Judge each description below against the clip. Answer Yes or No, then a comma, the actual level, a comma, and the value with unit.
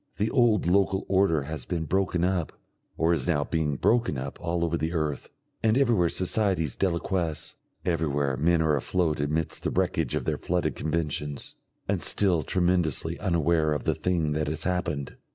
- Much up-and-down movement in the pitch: No, average, 3.2 semitones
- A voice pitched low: Yes, very low, 85 Hz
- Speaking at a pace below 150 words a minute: No, average, 170 wpm